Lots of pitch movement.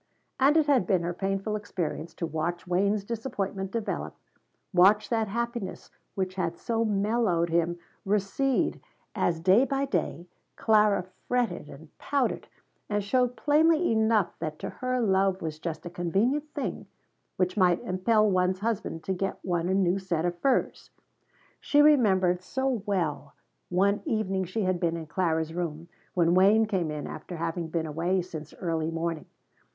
No: average, 4.4 semitones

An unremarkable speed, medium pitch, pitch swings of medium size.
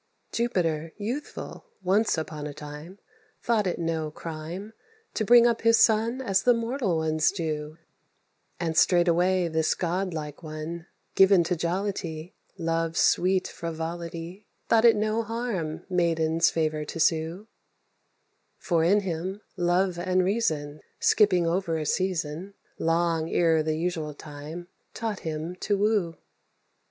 No: slow, 130 wpm; medium, 175 Hz; average, 3.6 semitones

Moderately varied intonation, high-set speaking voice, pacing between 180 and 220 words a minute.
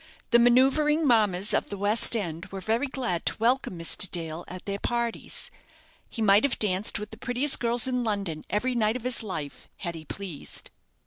Yes: average, 4.7 semitones; high, 215 Hz; average, 190 wpm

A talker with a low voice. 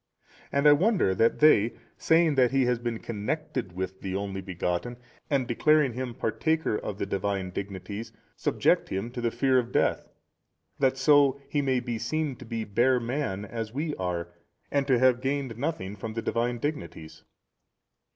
Yes: low, 120 Hz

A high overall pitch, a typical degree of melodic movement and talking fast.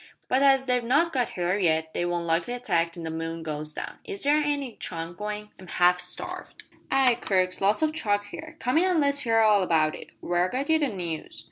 No: high, 205 Hz; wide, 7.7 semitones; fast, 225 wpm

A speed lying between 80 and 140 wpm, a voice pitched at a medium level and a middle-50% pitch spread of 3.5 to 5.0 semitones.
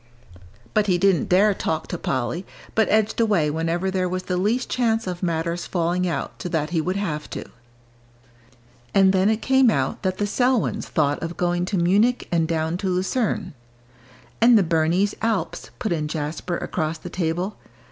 No: average, 175 wpm; medium, 180 Hz; average, 3.8 semitones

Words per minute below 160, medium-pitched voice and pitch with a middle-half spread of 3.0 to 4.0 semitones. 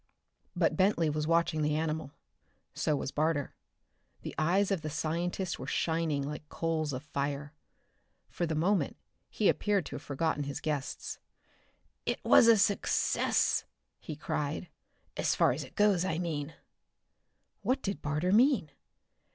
Yes: average, 145 wpm; medium, 160 Hz; average, 3.3 semitones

